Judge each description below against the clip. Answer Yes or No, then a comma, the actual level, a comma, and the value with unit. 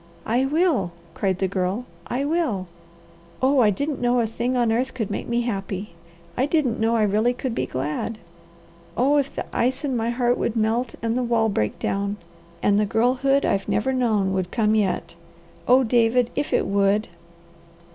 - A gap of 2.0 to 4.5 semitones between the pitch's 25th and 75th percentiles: Yes, average, 3.7 semitones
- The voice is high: Yes, high, 235 Hz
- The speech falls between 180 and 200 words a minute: Yes, average, 185 wpm